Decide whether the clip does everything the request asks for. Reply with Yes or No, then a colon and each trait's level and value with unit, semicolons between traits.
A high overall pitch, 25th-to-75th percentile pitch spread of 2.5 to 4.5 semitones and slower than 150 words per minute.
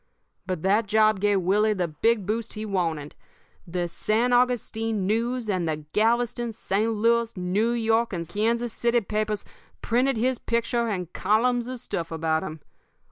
No: high, 215 Hz; average, 3.8 semitones; average, 155 wpm